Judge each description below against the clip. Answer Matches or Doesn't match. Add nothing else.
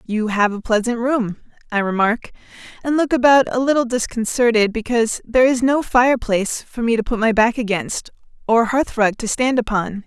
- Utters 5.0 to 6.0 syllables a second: Matches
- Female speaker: Matches